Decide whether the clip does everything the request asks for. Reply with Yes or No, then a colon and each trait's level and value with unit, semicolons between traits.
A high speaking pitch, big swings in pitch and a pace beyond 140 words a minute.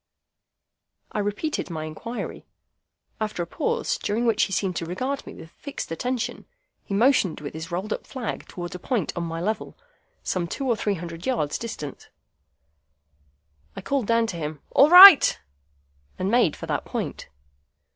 Yes: high, 205 Hz; wide, 6.3 semitones; average, 165 wpm